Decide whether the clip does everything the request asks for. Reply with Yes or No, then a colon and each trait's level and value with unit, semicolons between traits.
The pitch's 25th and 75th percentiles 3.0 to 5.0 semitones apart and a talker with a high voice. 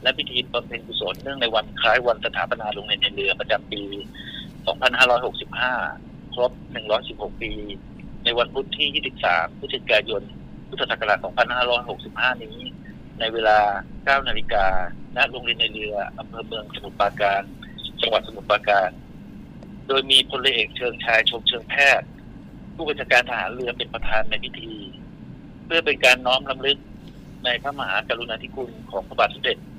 No: average, 3.9 semitones; low, 115 Hz